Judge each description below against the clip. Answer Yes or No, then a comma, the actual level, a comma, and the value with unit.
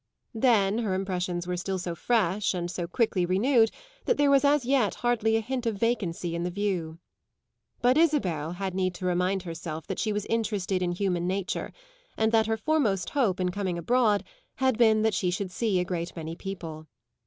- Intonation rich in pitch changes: No, average, 4.1 semitones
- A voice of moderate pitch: No, high, 195 Hz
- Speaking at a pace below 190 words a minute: No, average, 195 wpm